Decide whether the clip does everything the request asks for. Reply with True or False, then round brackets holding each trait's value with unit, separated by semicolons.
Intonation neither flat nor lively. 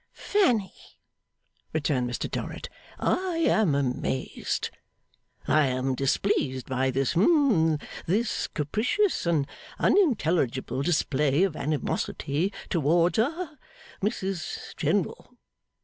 False (7.9 semitones)